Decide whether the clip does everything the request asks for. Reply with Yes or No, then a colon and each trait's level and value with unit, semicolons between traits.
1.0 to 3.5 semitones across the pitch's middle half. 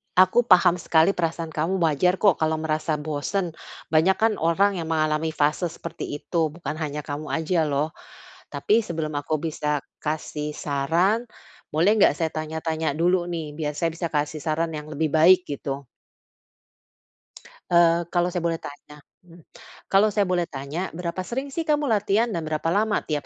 Yes: average, 2.8 semitones